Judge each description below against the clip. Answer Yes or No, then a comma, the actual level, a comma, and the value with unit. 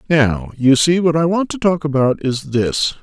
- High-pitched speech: No, medium, 150 Hz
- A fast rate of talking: Yes, fast, 220 wpm